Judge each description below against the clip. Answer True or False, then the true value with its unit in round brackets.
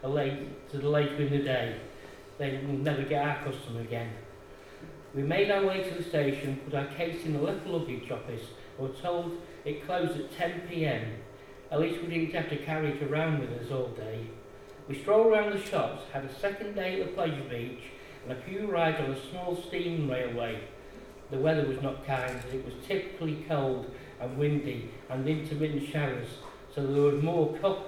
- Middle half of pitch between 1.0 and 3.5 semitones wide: False (4.1 semitones)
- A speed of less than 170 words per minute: False (200 wpm)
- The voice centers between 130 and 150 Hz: True (140 Hz)